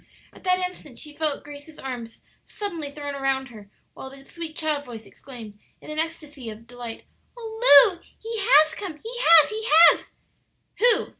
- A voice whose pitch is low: No, very high, 300 Hz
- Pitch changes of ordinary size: Yes, average, 4.5 semitones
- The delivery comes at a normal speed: Yes, average, 170 wpm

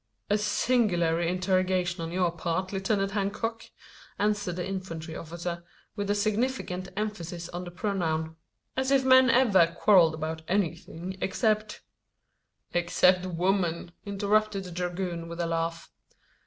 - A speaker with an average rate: No, slow, 130 wpm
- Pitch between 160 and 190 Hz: Yes, medium, 185 Hz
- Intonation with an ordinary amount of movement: Yes, average, 3.2 semitones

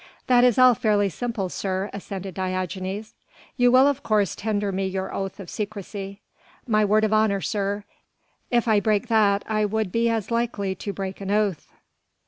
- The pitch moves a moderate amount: No, narrow, 2.2 semitones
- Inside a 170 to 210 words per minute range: Yes, average, 175 wpm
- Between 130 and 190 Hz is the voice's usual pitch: No, high, 205 Hz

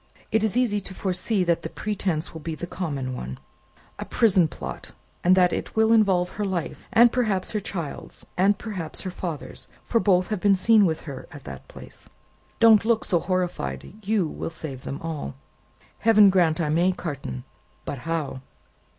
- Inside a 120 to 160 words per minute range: No, average, 180 wpm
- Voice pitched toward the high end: No, medium, 180 Hz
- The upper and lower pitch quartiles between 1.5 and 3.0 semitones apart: No, average, 4.6 semitones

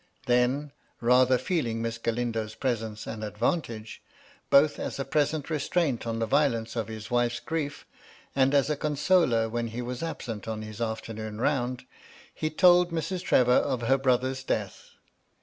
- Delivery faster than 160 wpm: No, average, 155 wpm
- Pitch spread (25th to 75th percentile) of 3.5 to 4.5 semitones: Yes, average, 4.1 semitones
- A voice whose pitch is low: Yes, low, 125 Hz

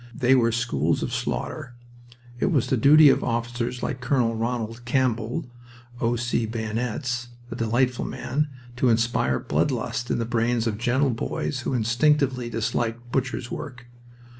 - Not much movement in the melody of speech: Yes, narrow, 1.8 semitones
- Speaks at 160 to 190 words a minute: No, average, 145 wpm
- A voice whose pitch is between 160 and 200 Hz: No, low, 120 Hz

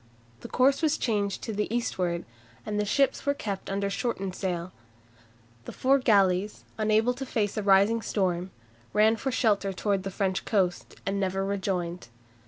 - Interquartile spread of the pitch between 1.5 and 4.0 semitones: Yes, average, 2.8 semitones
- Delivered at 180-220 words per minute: No, average, 165 wpm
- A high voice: Yes, high, 200 Hz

